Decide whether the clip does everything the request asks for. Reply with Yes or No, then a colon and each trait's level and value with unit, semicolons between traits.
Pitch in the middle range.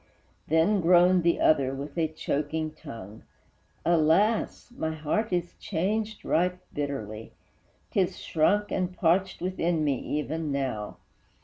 Yes: medium, 160 Hz